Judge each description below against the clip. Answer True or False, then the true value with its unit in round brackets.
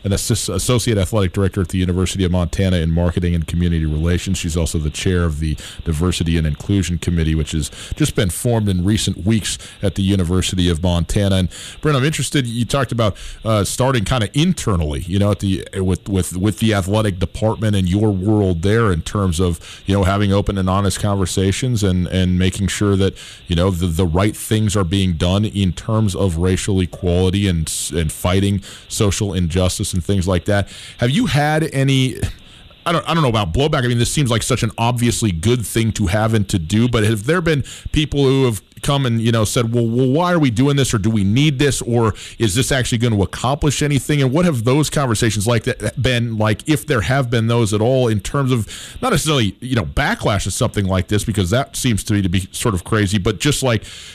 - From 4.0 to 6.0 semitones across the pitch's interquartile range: True (4.5 semitones)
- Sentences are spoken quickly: True (220 wpm)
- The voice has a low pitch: True (105 Hz)